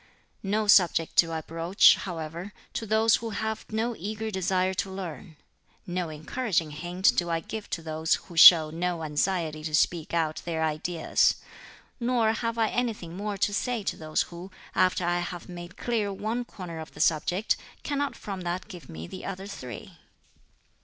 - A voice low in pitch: No, medium, 180 Hz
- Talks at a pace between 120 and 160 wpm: No, average, 175 wpm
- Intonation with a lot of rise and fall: No, average, 4.3 semitones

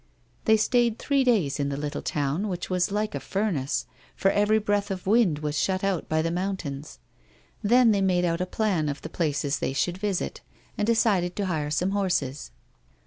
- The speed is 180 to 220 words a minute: Yes, average, 195 wpm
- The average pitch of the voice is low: No, medium, 185 Hz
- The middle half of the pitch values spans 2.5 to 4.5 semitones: No, average, 5.2 semitones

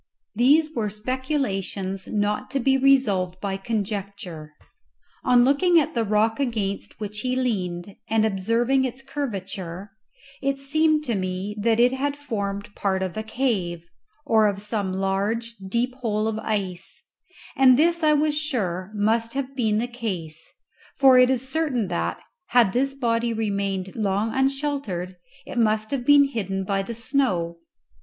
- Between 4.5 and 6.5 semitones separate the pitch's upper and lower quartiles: Yes, average, 5.1 semitones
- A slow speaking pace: No, average, 150 wpm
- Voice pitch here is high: Yes, high, 225 Hz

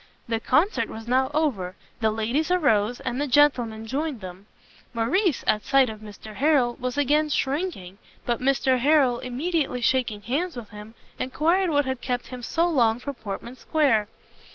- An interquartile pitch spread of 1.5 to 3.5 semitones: No, average, 4.8 semitones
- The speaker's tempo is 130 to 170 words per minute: Yes, average, 165 wpm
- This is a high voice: Yes, very high, 255 Hz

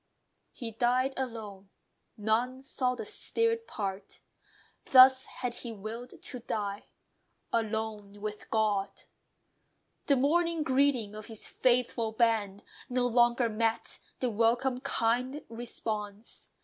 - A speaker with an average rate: No, slow, 110 wpm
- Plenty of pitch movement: No, average, 3.0 semitones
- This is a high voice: Yes, high, 235 Hz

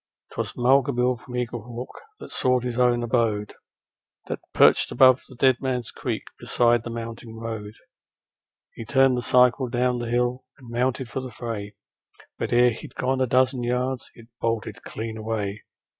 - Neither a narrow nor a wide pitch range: No, narrow, 1.7 semitones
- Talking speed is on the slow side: No, average, 165 wpm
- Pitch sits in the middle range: No, low, 120 Hz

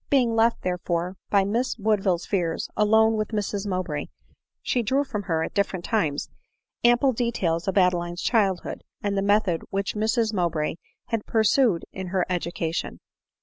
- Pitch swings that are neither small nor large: Yes, average, 3.9 semitones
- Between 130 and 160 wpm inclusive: Yes, average, 150 wpm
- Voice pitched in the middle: No, high, 200 Hz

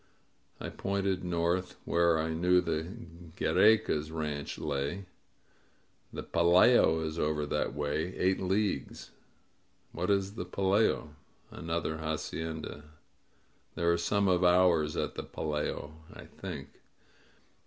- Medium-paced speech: No, slow, 120 wpm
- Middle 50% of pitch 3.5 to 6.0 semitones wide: No, average, 2.9 semitones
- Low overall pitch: Yes, very low, 85 Hz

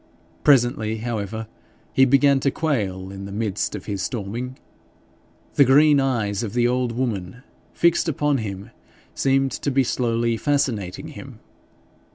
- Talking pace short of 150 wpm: Yes, average, 140 wpm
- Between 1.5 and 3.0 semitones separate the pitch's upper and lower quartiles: No, average, 4.6 semitones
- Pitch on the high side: No, low, 120 Hz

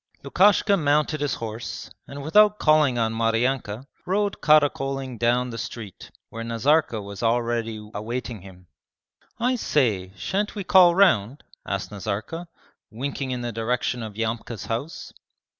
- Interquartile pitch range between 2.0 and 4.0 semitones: No, average, 5.2 semitones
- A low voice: Yes, low, 125 Hz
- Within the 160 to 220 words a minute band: No, slow, 135 wpm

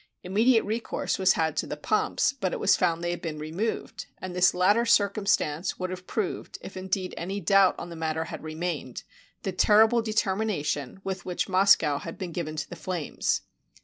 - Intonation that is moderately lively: Yes, average, 3.7 semitones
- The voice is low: No, medium, 185 Hz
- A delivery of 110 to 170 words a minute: No, average, 185 wpm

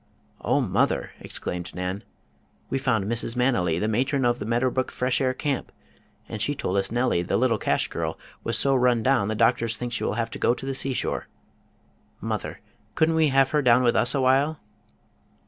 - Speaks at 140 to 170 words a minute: No, average, 195 wpm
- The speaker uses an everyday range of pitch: Yes, average, 3.2 semitones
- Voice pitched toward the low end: Yes, low, 125 Hz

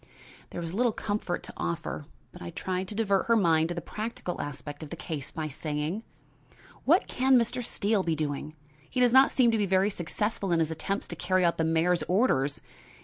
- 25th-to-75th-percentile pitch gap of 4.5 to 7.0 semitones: Yes, average, 4.8 semitones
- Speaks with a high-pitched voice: No, medium, 180 Hz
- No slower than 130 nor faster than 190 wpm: No, fast, 205 wpm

